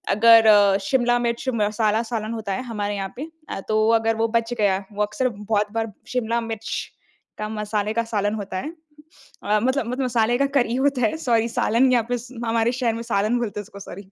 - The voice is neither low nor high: No, high, 225 Hz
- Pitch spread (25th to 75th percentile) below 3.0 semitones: Yes, narrow, 2.5 semitones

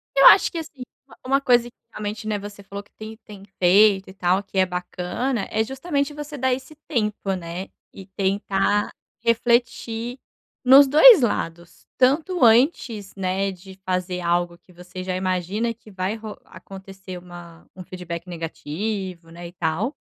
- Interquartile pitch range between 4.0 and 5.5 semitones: Yes, average, 4.5 semitones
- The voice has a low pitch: No, high, 200 Hz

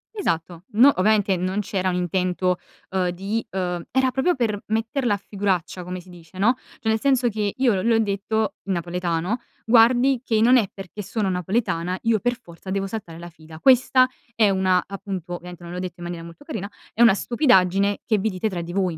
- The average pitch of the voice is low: No, high, 195 Hz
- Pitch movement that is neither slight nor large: Yes, average, 3.9 semitones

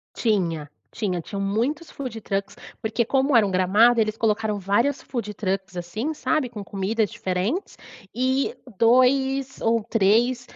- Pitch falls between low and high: No, high, 225 Hz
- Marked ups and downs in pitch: No, average, 4.4 semitones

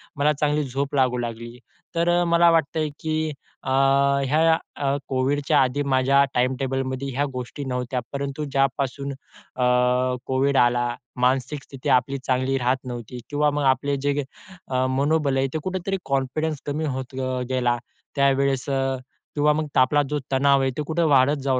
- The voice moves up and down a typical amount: No, narrow, 2.1 semitones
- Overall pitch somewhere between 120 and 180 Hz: Yes, low, 135 Hz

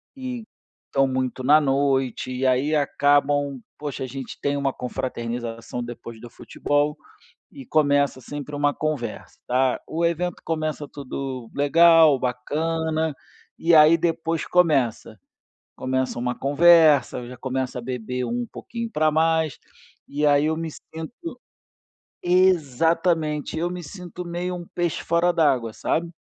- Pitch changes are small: No, average, 4.0 semitones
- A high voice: No, medium, 145 Hz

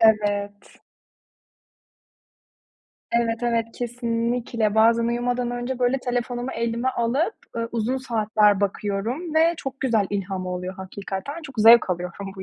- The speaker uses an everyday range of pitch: Yes, average, 3.2 semitones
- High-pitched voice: Yes, high, 230 Hz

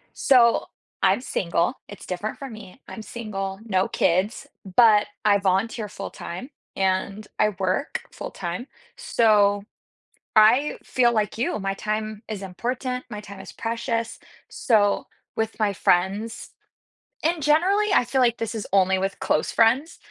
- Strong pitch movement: No, average, 3.4 semitones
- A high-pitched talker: Yes, high, 215 Hz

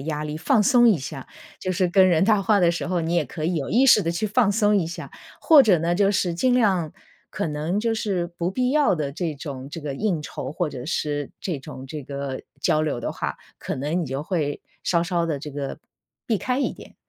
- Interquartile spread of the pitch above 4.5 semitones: Yes, average, 5.3 semitones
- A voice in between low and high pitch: Yes, medium, 170 Hz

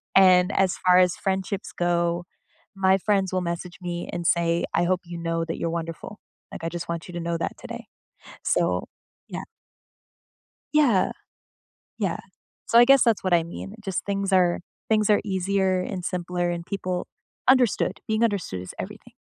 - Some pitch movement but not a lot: No, narrow, 2.3 semitones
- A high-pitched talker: No, medium, 180 Hz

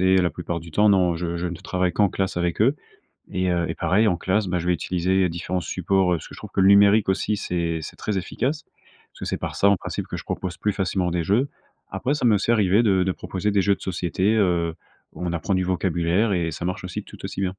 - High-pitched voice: No, very low, 95 Hz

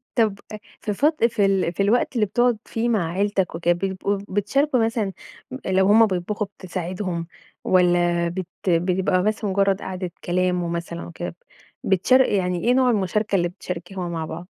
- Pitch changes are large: No, average, 3.2 semitones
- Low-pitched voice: No, high, 190 Hz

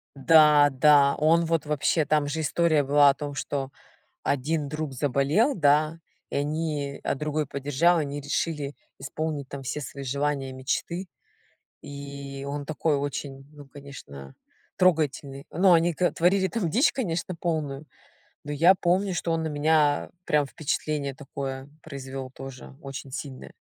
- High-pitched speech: No, medium, 145 Hz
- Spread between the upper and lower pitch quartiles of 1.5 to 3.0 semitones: Yes, narrow, 2.5 semitones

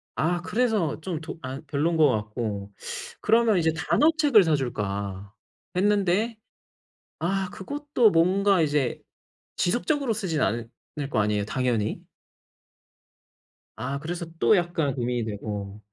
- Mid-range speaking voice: Yes, medium, 160 Hz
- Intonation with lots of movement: Yes, wide, 8.9 semitones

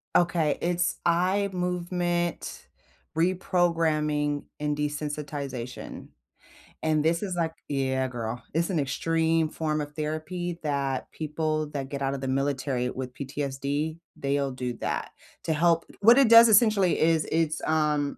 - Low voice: No, medium, 155 Hz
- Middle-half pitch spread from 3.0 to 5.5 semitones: Yes, average, 3.4 semitones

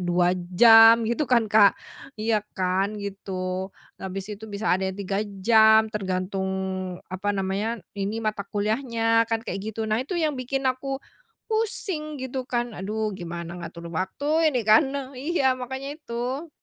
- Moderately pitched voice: No, high, 220 Hz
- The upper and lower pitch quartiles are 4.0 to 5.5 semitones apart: Yes, average, 4.7 semitones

